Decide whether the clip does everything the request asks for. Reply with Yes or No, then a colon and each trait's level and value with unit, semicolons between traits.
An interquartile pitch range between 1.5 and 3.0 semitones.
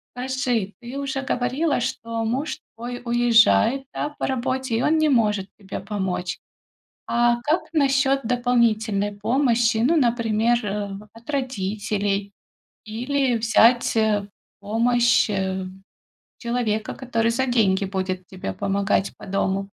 No: average, 3.5 semitones